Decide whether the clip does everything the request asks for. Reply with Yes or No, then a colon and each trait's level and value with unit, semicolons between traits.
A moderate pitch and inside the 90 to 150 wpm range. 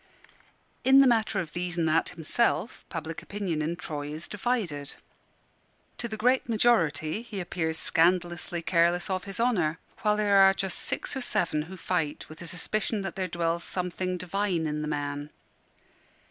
No: medium, 180 Hz; average, 165 wpm